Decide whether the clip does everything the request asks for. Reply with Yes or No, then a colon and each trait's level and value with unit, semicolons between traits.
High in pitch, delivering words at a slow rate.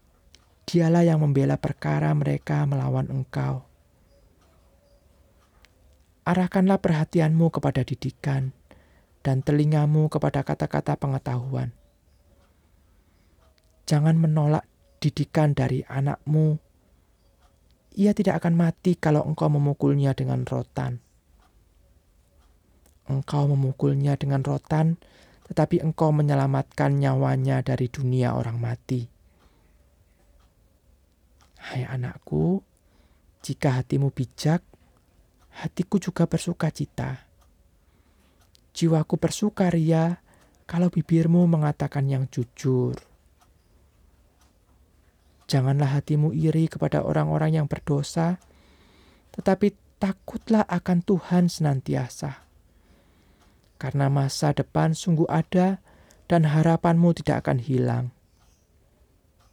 No: low, 130 Hz; slow, 80 wpm